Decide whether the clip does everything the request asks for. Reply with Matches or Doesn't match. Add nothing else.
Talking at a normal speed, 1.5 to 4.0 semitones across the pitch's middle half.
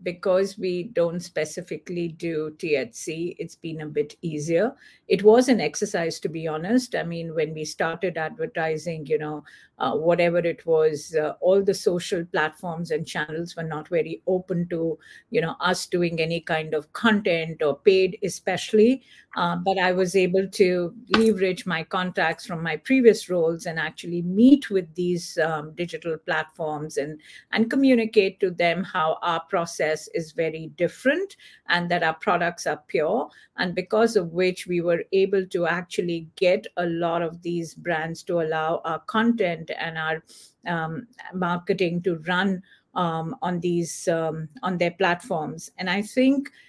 Matches